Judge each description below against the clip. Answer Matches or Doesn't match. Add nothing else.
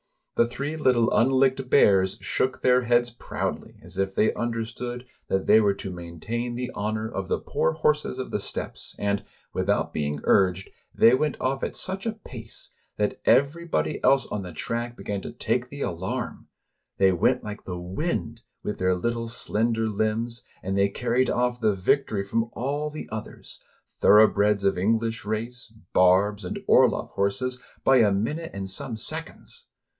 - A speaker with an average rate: Matches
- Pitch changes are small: Doesn't match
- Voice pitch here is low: Matches